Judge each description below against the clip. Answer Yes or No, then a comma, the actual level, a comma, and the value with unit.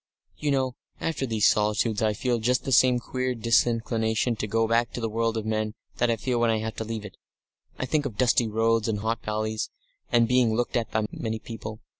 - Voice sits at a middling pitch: No, low, 115 Hz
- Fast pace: Yes, fast, 220 wpm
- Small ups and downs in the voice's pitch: Yes, narrow, 1.8 semitones